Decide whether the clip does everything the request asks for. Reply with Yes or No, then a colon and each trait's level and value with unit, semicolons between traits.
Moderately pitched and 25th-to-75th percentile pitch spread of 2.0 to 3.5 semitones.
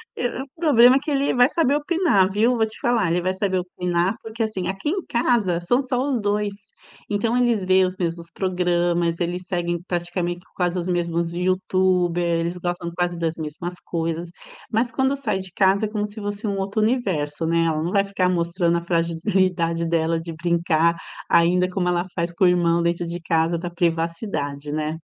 Yes: medium, 180 Hz; average, 3.2 semitones